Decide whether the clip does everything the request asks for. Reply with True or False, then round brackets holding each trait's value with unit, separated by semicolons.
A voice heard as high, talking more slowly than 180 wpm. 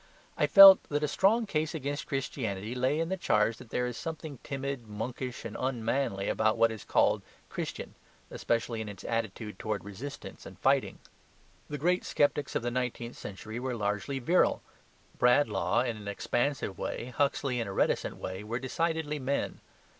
False (125 Hz; 170 wpm)